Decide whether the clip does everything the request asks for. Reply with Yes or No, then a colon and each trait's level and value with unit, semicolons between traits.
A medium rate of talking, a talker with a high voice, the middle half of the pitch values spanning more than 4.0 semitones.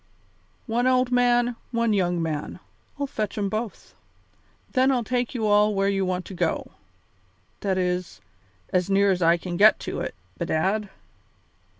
Yes: average, 165 wpm; high, 200 Hz; average, 4.7 semitones